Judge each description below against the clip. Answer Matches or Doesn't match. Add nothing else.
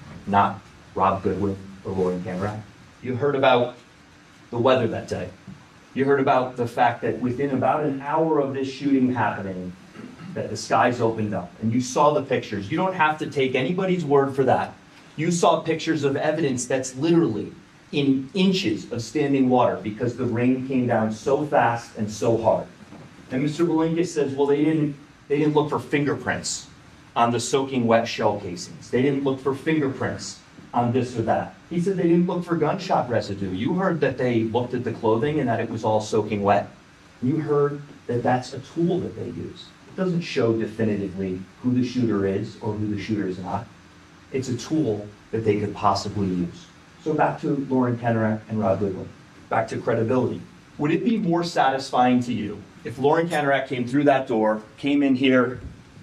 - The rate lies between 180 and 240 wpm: Matches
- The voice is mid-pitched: Doesn't match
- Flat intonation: Doesn't match